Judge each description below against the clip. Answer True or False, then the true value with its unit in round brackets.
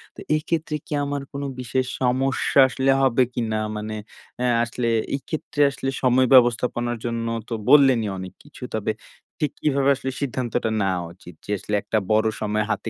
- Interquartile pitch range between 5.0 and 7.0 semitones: False (3.4 semitones)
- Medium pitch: False (125 Hz)